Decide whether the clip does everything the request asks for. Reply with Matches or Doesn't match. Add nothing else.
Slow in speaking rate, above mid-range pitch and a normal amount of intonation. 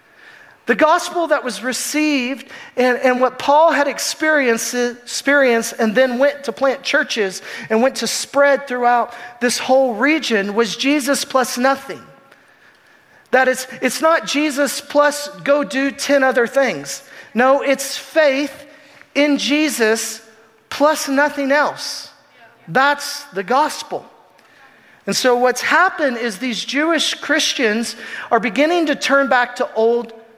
Matches